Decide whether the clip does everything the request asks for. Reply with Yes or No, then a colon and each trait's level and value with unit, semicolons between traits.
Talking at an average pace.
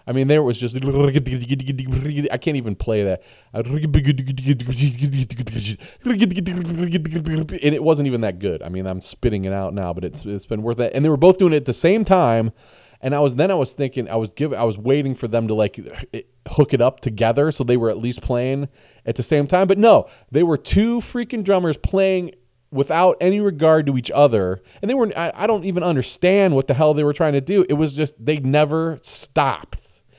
No: fast, 215 wpm